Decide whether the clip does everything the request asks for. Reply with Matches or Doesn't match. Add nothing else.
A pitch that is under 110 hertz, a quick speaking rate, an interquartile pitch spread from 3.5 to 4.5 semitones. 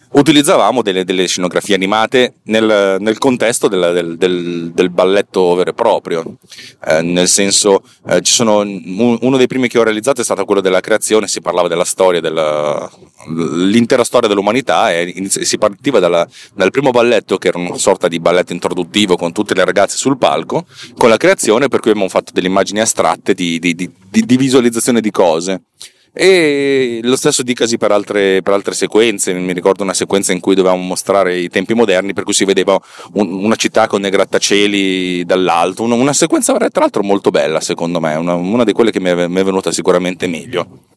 Matches